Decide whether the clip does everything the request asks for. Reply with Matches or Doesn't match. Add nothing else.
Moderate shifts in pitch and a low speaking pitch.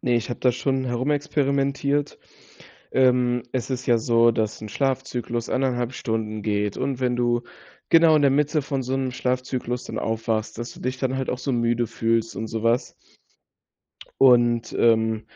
Doesn't match